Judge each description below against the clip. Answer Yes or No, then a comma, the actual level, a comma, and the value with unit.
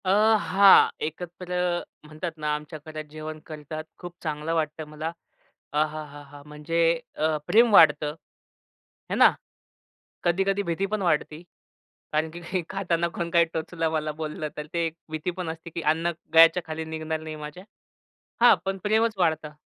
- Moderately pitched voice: Yes, medium, 160 Hz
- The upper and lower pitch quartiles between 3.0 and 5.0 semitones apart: No, narrow, 2.4 semitones